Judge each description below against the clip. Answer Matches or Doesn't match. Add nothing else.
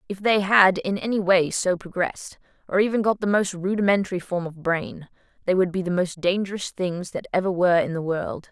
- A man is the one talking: Doesn't match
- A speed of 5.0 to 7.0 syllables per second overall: Matches